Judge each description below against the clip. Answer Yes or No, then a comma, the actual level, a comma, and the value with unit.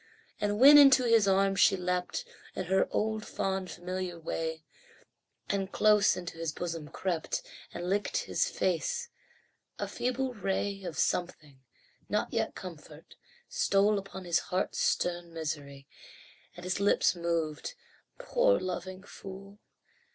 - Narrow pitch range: No, average, 3.3 semitones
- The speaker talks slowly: Yes, slow, 130 wpm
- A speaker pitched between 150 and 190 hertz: Yes, medium, 185 Hz